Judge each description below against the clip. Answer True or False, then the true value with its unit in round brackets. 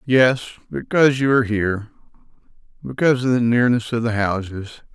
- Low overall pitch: True (115 Hz)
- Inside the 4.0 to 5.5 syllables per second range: False (5.9 syllables/s)